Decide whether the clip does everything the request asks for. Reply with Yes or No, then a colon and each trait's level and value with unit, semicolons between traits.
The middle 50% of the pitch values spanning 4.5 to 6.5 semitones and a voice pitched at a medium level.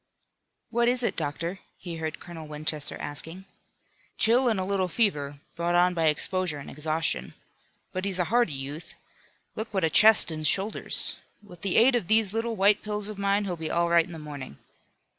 Yes: average, 4.8 semitones; medium, 180 Hz